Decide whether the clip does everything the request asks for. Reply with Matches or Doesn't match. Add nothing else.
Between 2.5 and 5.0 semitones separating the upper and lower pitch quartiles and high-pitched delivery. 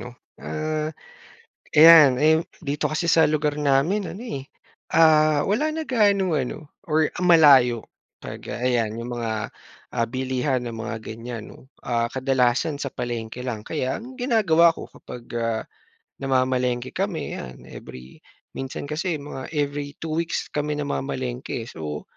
Doesn't match